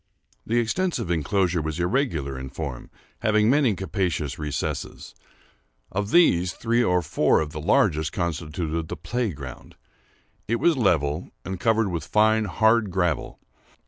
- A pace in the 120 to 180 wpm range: Yes, average, 140 wpm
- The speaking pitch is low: Yes, very low, 90 Hz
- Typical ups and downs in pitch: No, wide, 5.8 semitones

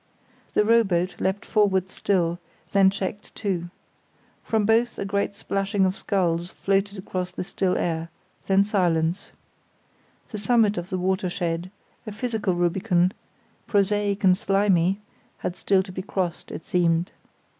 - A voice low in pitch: No, high, 190 Hz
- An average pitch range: No, narrow, 2.3 semitones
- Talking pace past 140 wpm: No, slow, 135 wpm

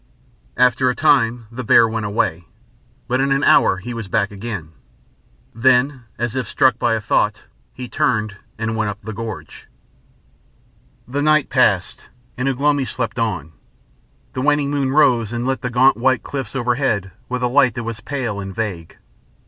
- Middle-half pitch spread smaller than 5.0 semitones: Yes, average, 3.2 semitones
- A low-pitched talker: Yes, low, 120 Hz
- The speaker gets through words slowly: No, average, 175 wpm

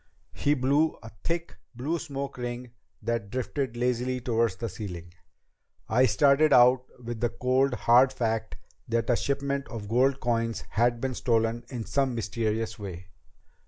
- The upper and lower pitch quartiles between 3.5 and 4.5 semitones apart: No, average, 2.7 semitones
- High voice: No, low, 120 Hz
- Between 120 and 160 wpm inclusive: Yes, average, 150 wpm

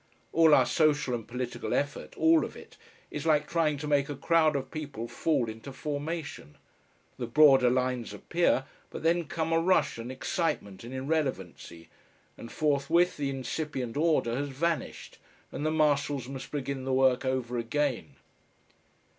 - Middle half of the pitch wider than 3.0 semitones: Yes, average, 3.5 semitones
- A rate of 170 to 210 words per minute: No, average, 155 wpm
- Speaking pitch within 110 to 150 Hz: Yes, medium, 140 Hz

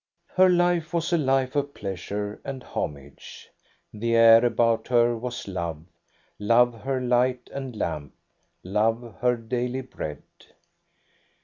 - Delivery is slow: Yes, slow, 130 wpm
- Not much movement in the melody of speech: No, average, 3.8 semitones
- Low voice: Yes, low, 120 Hz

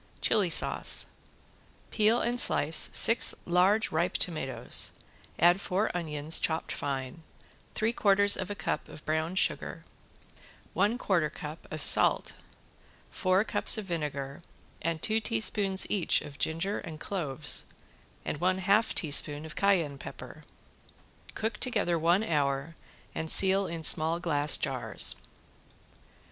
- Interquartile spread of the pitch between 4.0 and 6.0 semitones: Yes, average, 4.6 semitones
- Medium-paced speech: No, slow, 130 wpm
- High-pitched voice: No, medium, 170 Hz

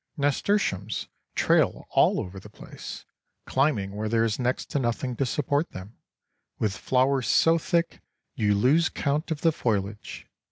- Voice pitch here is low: Yes, low, 125 Hz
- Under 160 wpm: Yes, average, 150 wpm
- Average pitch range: No, wide, 5.7 semitones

